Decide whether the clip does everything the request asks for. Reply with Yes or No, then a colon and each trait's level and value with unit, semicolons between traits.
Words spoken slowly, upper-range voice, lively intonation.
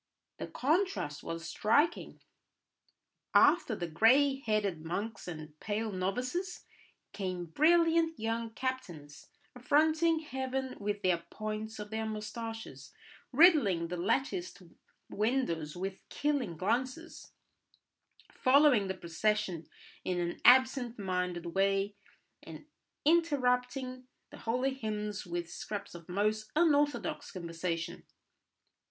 Yes: slow, 105 wpm; high, 220 Hz; wide, 6.5 semitones